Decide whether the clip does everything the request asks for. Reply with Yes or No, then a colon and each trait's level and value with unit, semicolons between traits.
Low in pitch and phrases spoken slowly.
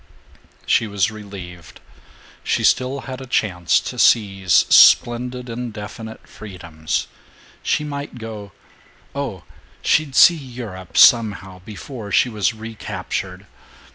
Yes: low, 110 Hz; slow, 110 wpm